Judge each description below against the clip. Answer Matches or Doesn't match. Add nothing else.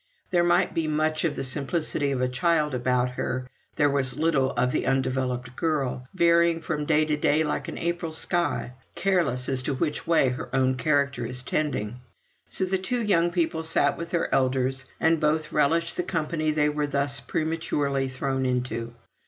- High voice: Doesn't match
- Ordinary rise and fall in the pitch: Matches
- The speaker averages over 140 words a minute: Matches